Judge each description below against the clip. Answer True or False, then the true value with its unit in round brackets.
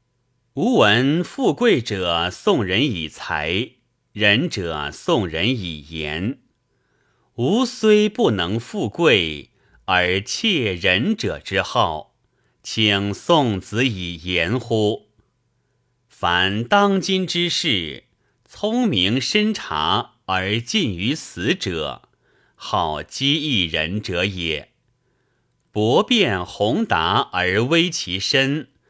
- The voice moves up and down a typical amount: False (8.0 semitones)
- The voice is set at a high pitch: False (120 Hz)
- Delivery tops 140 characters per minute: False (125 characters per minute)